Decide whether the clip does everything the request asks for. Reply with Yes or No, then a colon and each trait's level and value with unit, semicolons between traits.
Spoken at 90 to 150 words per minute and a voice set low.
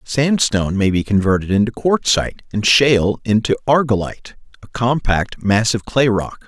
Yes: average, 140 wpm; low, 115 Hz